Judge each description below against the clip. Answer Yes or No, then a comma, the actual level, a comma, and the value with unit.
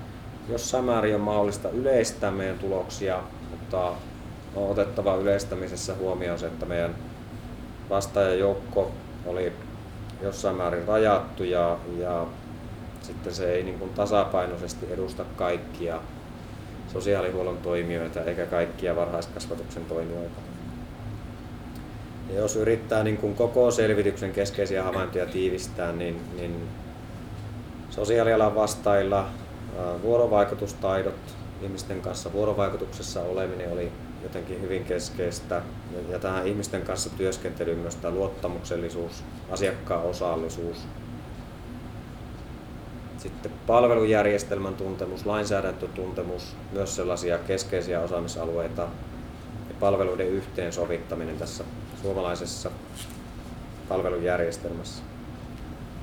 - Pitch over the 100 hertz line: No, very low, 95 Hz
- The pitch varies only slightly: No, average, 3.7 semitones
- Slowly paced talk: Yes, slow, 90 wpm